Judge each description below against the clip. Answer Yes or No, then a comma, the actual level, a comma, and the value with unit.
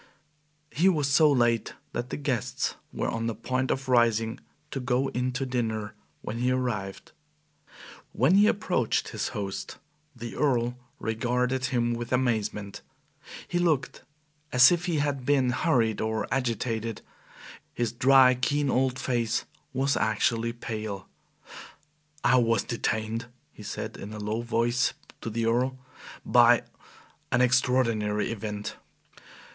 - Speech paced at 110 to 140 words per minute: Yes, slow, 135 wpm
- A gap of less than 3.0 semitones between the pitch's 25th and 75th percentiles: Yes, narrow, 2.6 semitones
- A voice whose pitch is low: Yes, low, 120 Hz